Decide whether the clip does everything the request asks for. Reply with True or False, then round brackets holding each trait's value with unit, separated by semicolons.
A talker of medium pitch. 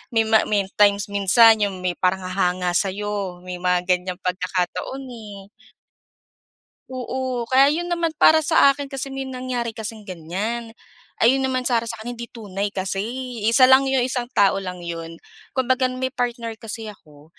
False (220 Hz)